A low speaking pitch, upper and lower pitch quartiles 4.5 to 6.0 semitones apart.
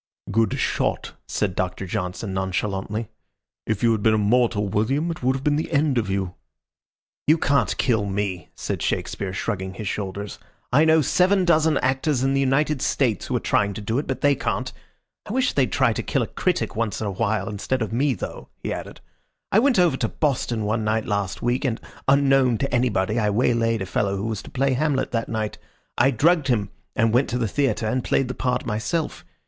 Yes: low, 115 Hz; average, 4.9 semitones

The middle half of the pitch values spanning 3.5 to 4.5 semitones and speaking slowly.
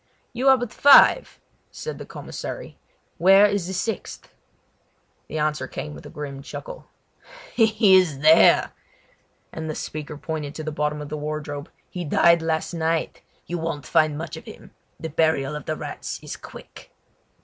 No: average, 3.8 semitones; average, 165 wpm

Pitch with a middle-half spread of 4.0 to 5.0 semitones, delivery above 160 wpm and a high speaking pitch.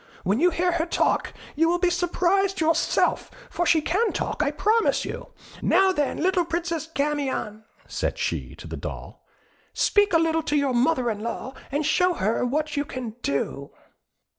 Yes: average, 4.3 semitones; average, 175 wpm; very high, 320 Hz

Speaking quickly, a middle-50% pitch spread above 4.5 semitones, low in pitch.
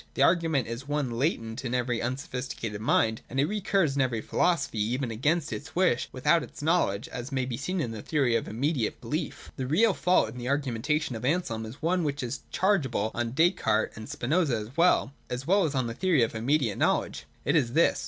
Yes: fast, 210 wpm; wide, 5.4 semitones; low, 130 Hz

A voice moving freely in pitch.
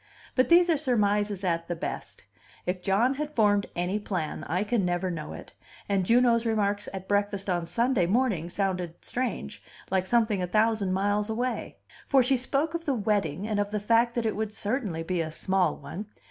No: average, 4.2 semitones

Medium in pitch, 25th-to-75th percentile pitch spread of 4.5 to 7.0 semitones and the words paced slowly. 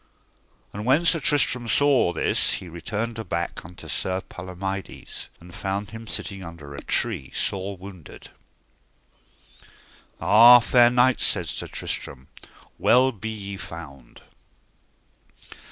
No: low, 100 Hz; average, 5.2 semitones; slow, 120 wpm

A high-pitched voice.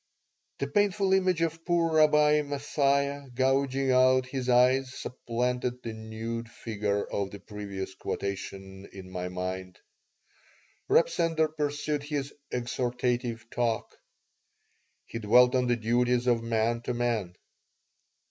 No: low, 125 Hz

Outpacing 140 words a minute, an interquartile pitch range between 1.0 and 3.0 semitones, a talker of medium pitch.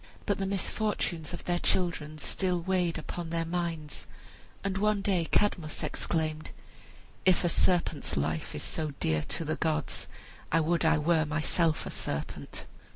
Yes: average, 155 wpm; narrow, 2.6 semitones; medium, 165 Hz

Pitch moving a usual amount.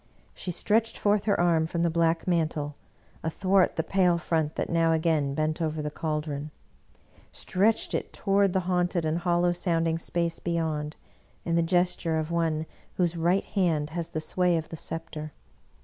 No: narrow, 2.0 semitones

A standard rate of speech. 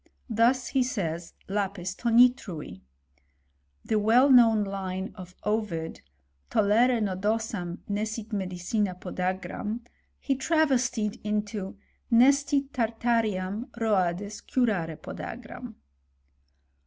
No: slow, 90 wpm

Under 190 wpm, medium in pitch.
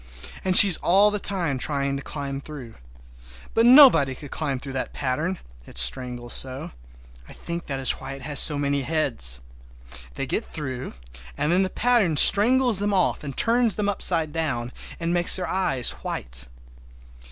Yes: average, 170 wpm; medium, 150 Hz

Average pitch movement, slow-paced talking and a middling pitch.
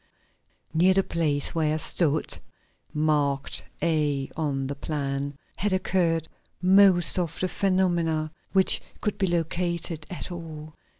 Yes: average, 3.2 semitones; slow, 130 wpm; medium, 165 Hz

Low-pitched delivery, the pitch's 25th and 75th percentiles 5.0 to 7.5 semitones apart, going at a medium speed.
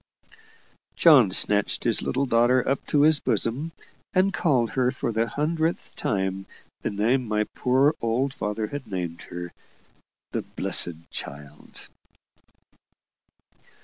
No: low, 120 Hz; wide, 5.5 semitones; slow, 120 wpm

